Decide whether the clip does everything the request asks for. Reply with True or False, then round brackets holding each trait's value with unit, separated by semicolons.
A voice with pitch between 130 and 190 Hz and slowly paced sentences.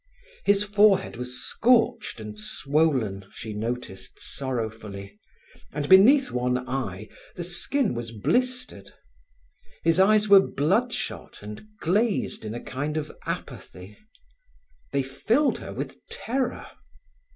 True (140 Hz; 115 wpm)